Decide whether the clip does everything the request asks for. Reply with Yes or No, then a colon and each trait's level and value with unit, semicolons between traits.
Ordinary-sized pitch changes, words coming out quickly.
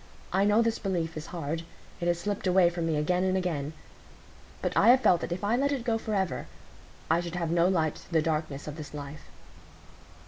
Yes: average, 3.4 semitones; fast, 215 wpm